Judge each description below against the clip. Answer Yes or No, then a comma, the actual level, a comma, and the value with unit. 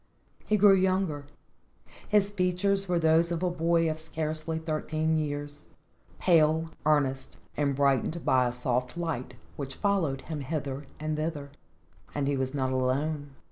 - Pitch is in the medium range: Yes, medium, 155 Hz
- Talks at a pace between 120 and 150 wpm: Yes, average, 145 wpm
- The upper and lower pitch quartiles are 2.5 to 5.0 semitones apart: Yes, average, 3.2 semitones